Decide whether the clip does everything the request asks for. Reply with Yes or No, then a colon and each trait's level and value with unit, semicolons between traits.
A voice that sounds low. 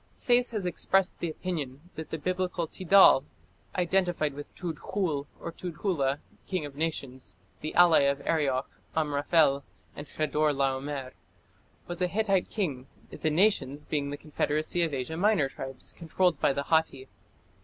No: medium, 155 Hz